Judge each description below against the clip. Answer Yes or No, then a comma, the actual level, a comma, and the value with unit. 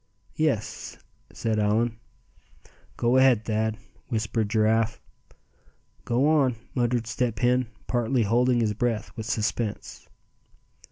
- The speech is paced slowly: Yes, slow, 105 wpm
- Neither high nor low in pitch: No, low, 115 Hz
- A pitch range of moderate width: No, narrow, 2.1 semitones